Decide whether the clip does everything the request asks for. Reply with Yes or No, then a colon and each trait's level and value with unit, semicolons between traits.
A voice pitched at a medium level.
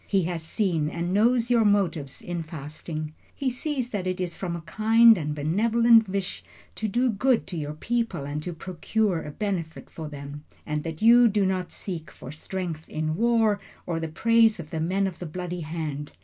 Yes: medium, 180 Hz